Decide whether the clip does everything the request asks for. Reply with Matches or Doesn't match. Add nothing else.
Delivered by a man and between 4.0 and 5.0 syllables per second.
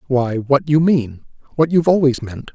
Matches